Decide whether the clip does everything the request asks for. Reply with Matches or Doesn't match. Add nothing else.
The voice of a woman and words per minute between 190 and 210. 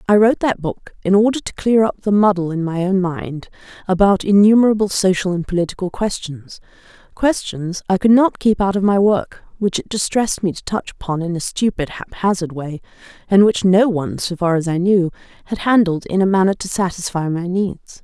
Matches